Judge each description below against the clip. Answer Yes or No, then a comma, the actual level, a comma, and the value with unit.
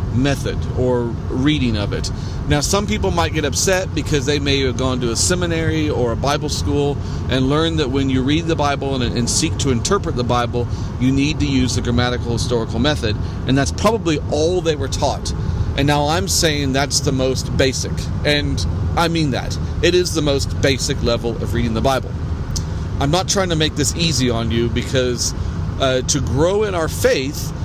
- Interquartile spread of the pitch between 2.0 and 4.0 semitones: No, average, 5.3 semitones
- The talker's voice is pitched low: Yes, low, 120 Hz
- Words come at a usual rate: Yes, average, 195 wpm